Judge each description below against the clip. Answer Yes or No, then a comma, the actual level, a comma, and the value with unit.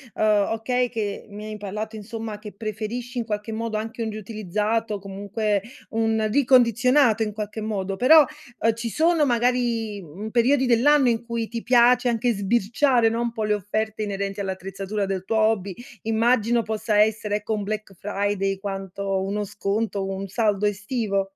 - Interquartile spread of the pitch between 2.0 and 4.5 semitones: Yes, narrow, 2.4 semitones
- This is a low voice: No, high, 215 Hz